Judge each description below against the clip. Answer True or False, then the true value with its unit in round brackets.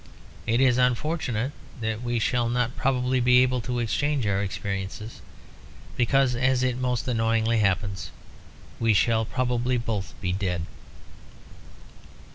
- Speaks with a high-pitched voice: False (120 Hz)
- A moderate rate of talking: False (125 wpm)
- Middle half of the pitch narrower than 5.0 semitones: True (2.5 semitones)